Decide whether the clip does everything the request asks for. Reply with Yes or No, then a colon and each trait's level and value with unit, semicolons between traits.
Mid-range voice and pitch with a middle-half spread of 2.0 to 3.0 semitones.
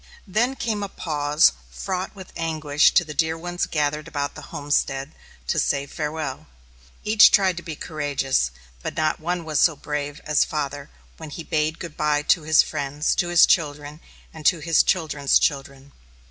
Yes: medium, 155 Hz; narrow, 2.5 semitones